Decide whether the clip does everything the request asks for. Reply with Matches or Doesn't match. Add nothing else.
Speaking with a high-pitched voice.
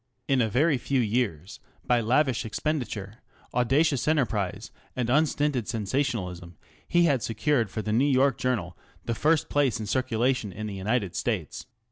Doesn't match